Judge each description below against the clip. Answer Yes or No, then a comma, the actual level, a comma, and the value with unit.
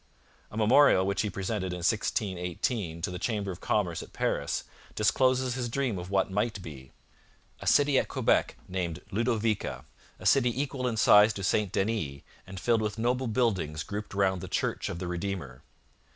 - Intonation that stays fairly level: No, average, 4.4 semitones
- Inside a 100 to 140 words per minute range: No, average, 175 wpm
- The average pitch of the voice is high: No, low, 105 Hz